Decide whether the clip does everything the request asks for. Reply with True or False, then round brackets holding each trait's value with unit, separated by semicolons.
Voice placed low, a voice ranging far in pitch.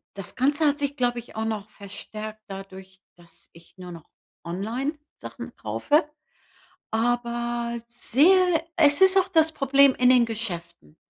False (235 Hz; 6.4 semitones)